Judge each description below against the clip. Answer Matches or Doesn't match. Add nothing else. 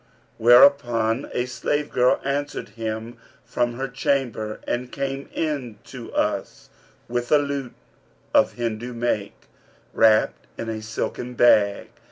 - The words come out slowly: Matches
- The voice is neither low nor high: Doesn't match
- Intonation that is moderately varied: Matches